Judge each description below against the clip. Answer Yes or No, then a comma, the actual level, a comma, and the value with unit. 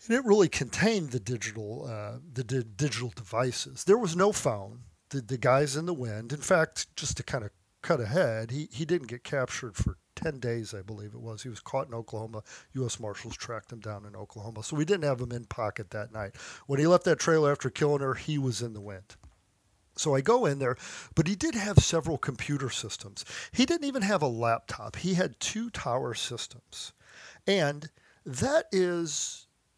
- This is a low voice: Yes, low, 130 Hz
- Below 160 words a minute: No, fast, 205 wpm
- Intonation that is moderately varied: No, wide, 6.3 semitones